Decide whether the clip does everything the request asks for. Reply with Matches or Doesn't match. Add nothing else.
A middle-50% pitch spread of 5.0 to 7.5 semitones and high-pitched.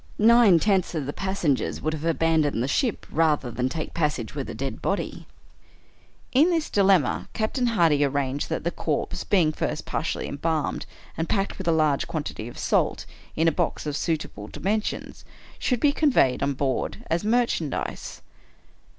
Doesn't match